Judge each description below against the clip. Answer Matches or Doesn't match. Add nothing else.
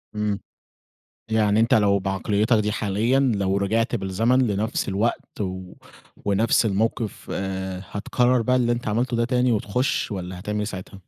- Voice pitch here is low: Matches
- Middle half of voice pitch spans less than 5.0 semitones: Matches